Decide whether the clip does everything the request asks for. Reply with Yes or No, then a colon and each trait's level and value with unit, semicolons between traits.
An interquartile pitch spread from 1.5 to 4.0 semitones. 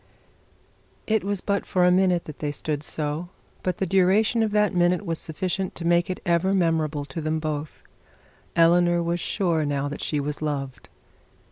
Yes: average, 3.4 semitones